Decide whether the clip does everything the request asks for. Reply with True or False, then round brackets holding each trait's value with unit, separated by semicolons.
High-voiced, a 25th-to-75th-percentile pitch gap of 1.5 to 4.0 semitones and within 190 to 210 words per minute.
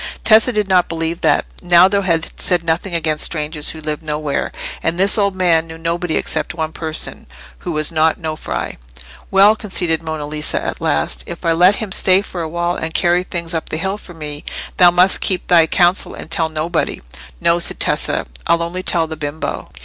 False (170 Hz; 2.4 semitones; 195 wpm)